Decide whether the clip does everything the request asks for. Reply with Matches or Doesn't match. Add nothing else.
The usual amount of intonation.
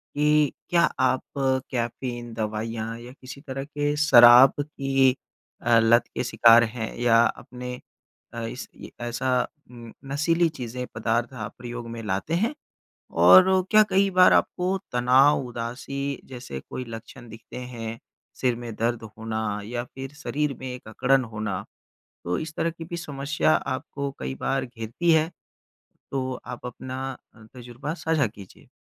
Matches